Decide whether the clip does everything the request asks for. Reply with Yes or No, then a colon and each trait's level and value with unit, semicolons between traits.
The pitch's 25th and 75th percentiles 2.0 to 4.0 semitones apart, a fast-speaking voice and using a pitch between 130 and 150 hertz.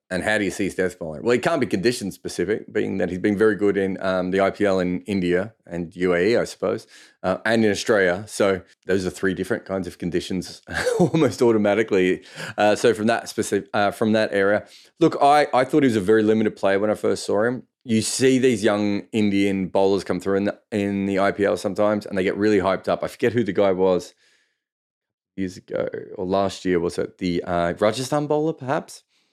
No: average, 2.9 semitones; fast, 215 wpm; low, 100 Hz